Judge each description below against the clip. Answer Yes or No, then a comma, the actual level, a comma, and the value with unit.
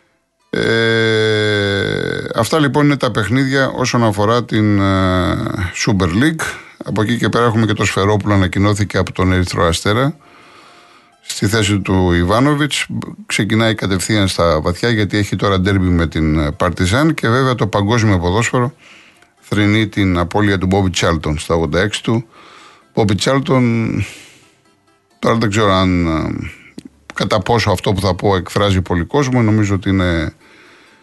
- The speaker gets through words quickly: No, average, 140 wpm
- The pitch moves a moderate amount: Yes, average, 3.5 semitones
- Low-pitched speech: Yes, low, 105 Hz